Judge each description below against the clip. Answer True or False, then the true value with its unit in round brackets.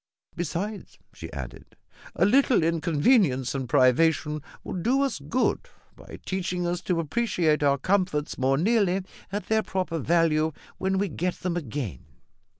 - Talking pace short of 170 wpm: True (145 wpm)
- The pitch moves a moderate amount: True (4.5 semitones)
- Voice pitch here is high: False (175 Hz)